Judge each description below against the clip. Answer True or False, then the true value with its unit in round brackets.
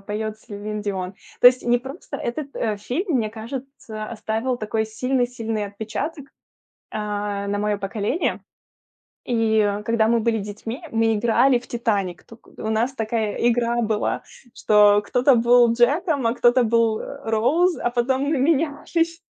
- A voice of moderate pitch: False (230 Hz)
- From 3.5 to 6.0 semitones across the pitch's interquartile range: False (2.9 semitones)